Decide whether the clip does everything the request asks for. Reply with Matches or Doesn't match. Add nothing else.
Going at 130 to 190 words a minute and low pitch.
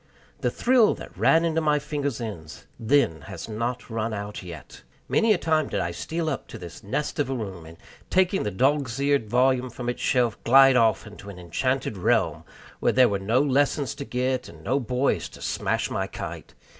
Doesn't match